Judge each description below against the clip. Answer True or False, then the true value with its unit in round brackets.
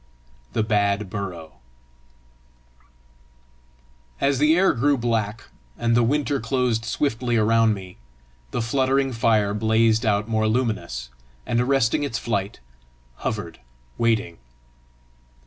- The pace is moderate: False (110 wpm)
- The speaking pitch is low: True (115 Hz)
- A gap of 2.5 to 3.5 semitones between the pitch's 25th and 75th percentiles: True (3.2 semitones)